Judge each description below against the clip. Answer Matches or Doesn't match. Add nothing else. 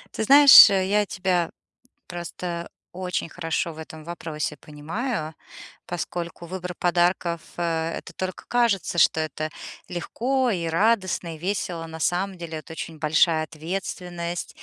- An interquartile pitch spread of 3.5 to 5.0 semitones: Doesn't match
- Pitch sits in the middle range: Matches